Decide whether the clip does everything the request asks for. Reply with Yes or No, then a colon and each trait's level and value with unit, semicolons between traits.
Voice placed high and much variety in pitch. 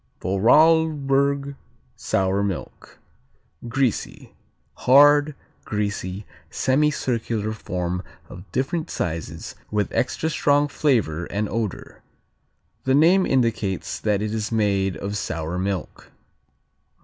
No: low, 110 Hz; wide, 6.3 semitones